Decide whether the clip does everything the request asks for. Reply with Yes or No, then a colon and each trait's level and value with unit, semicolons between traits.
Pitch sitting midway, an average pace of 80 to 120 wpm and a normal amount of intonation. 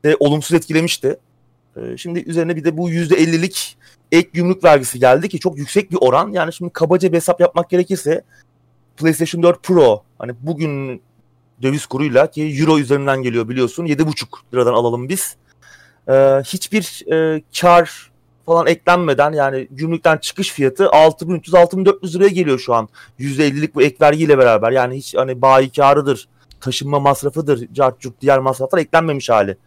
No: medium, 155 Hz; fast, 140 wpm; average, 4.5 semitones